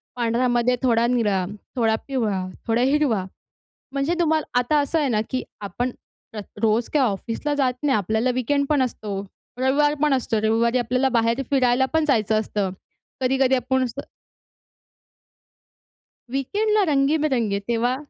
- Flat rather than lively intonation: No, average, 3.4 semitones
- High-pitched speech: Yes, very high, 250 Hz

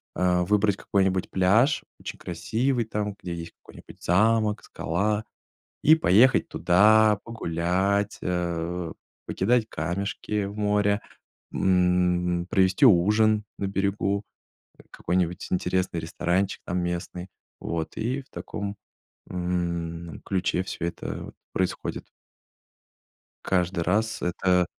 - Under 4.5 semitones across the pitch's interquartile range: Yes, average, 2.9 semitones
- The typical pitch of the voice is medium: No, very low, 95 Hz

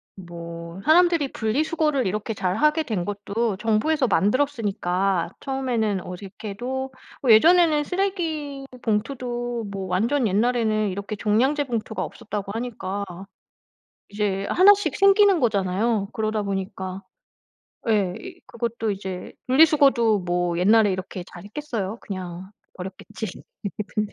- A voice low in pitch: No, high, 220 Hz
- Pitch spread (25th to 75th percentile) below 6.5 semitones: Yes, wide, 5.6 semitones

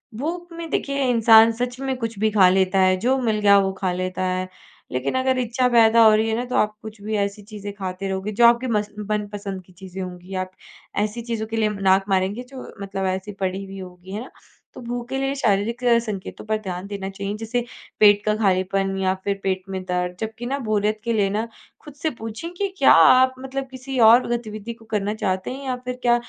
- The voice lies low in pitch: No, high, 215 Hz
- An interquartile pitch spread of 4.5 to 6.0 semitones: No, average, 3.7 semitones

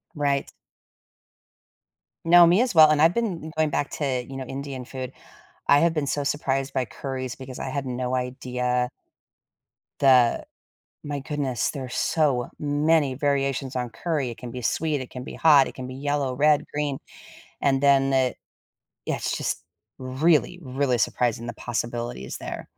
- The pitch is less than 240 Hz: Yes, low, 135 Hz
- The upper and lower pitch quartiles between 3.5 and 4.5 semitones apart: No, narrow, 2.5 semitones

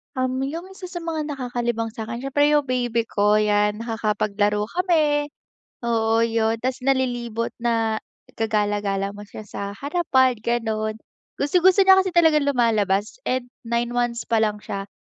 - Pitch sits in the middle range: No, high, 235 Hz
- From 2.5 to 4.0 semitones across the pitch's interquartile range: No, average, 4.5 semitones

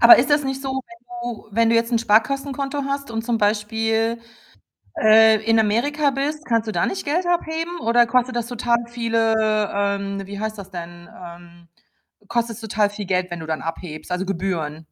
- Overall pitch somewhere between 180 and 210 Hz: No, high, 225 Hz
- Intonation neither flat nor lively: Yes, average, 3.4 semitones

